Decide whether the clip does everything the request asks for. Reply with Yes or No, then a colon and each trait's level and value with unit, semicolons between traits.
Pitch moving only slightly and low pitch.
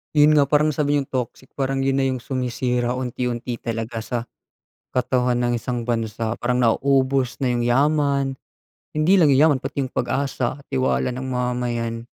Yes: narrow, 2.2 semitones; low, 125 Hz